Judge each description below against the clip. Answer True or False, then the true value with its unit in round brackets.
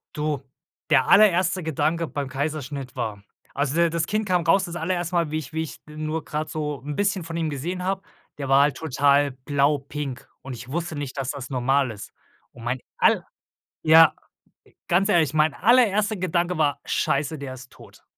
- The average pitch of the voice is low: False (155 Hz)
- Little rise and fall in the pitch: False (3.6 semitones)